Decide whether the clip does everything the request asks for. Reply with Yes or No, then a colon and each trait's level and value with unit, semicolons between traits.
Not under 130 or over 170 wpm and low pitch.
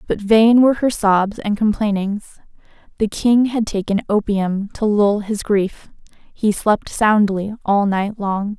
No: average, 155 wpm; high, 210 Hz